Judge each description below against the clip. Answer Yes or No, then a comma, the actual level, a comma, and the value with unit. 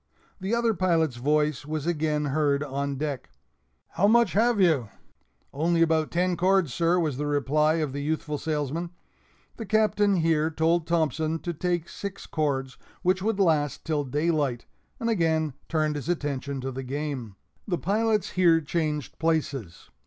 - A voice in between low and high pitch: Yes, medium, 155 Hz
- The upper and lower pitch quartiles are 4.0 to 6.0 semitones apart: No, average, 3.2 semitones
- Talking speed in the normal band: Yes, average, 155 wpm